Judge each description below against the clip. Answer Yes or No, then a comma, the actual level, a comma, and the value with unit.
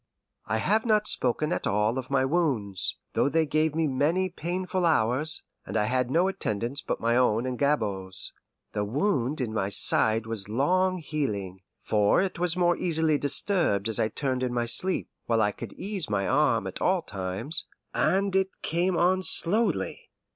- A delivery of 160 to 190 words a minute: Yes, average, 175 wpm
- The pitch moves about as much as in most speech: No, wide, 7.9 semitones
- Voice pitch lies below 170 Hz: Yes, medium, 140 Hz